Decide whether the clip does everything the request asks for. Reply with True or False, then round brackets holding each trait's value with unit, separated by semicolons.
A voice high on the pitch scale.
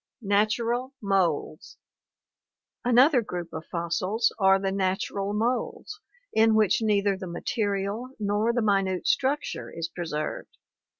True (200 Hz)